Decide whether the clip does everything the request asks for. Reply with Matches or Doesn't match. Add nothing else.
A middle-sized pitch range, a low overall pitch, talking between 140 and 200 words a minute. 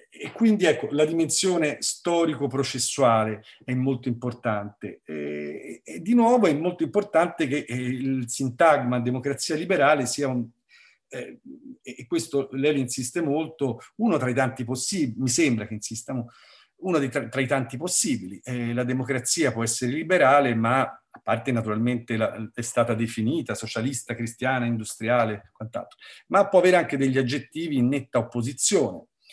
Matches